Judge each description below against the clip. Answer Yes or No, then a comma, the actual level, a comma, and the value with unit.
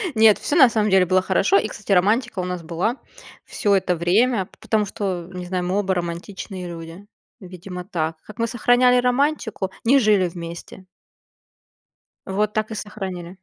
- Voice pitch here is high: Yes, high, 195 Hz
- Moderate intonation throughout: Yes, average, 3.4 semitones